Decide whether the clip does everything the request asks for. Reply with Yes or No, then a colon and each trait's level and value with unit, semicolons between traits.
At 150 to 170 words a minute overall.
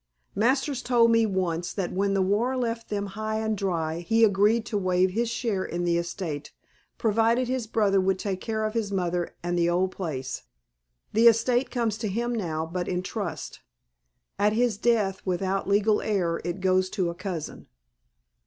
No: average, 180 wpm